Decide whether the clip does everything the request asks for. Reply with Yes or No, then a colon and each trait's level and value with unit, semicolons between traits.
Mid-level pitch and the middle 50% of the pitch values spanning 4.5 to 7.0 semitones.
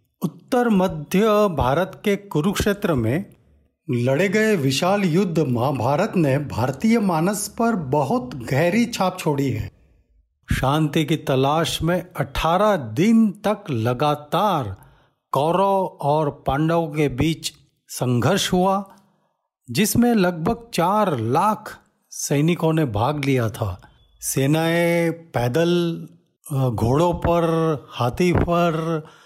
Yes: medium, 160 Hz; wide, 5.6 semitones